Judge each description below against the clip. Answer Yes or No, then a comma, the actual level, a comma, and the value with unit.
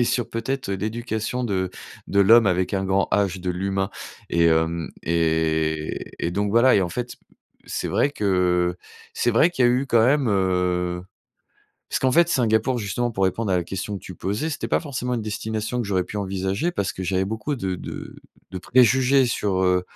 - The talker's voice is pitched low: Yes, low, 100 Hz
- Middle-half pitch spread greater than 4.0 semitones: Yes, average, 4.7 semitones